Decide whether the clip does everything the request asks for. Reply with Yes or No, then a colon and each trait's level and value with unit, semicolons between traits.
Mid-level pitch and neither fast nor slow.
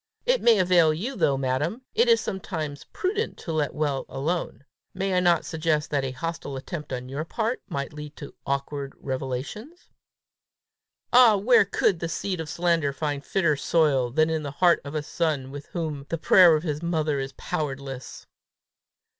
Yes: medium, 155 Hz; average, 170 wpm